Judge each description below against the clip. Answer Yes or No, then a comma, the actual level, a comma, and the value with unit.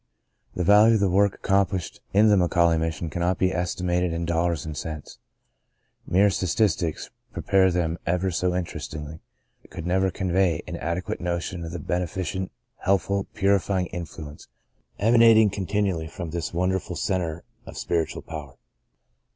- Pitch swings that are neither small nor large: No, narrow, 2.3 semitones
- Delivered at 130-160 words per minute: Yes, average, 150 wpm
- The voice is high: No, very low, 90 Hz